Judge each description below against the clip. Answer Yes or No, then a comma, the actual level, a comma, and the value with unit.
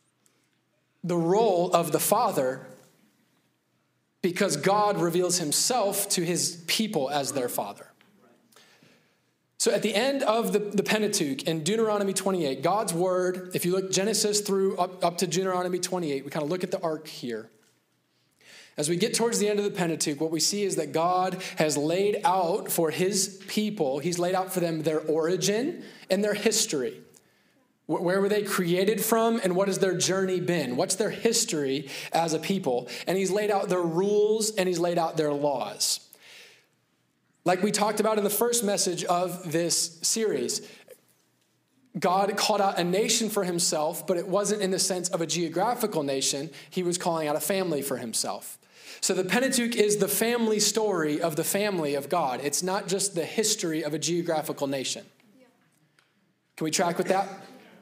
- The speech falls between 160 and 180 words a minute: Yes, average, 175 wpm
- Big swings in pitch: No, average, 3.8 semitones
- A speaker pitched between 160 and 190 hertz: Yes, medium, 185 Hz